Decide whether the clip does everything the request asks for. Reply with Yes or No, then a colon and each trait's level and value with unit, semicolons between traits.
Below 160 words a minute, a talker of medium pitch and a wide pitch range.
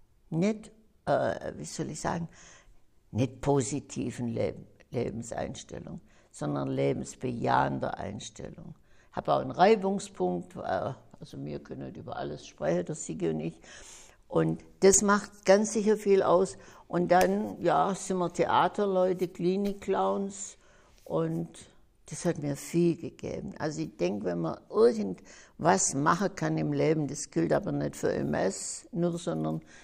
Yes: average, 135 wpm; medium, 170 Hz; wide, 8.2 semitones